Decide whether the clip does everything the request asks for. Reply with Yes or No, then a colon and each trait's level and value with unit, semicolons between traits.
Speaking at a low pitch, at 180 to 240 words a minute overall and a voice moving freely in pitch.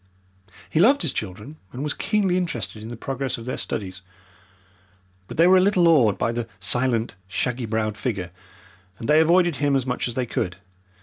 Yes: low, 125 Hz; average, 190 wpm; wide, 6.5 semitones